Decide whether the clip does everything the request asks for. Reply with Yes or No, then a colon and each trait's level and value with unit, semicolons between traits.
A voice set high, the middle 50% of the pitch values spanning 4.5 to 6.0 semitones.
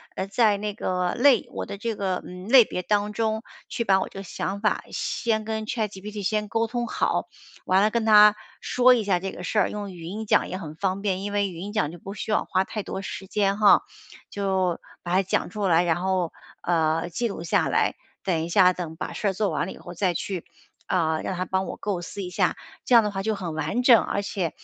No: high, 195 Hz; average, 2.7 semitones